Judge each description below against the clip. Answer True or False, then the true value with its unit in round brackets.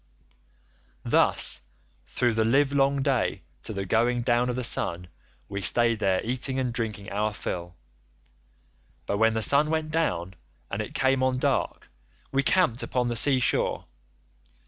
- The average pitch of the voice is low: True (120 Hz)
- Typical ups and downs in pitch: True (3.8 semitones)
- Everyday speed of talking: True (150 wpm)